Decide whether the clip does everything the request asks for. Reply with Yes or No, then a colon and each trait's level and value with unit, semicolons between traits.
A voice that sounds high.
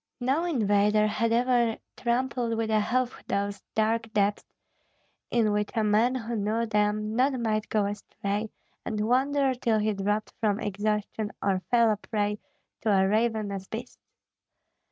Yes: high, 215 Hz